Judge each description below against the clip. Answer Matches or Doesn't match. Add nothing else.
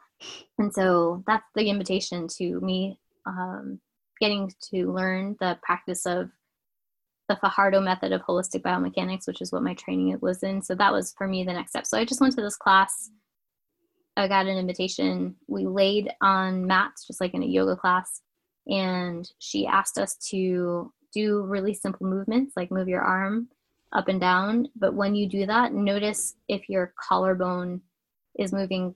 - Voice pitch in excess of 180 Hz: Matches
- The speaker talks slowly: Doesn't match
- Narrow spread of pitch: Matches